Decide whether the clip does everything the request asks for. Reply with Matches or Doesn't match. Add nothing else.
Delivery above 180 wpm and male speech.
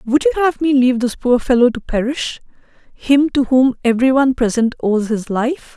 Doesn't match